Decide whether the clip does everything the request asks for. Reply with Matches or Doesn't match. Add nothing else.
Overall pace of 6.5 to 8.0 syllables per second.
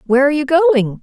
Matches